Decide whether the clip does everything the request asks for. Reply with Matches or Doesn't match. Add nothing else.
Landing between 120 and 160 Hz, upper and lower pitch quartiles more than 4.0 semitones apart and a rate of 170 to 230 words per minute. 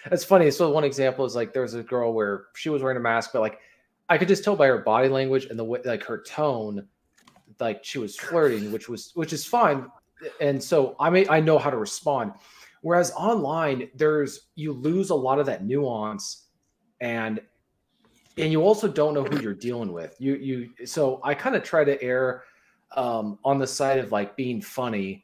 Matches